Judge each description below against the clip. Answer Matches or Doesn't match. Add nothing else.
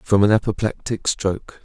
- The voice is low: Matches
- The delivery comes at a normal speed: Matches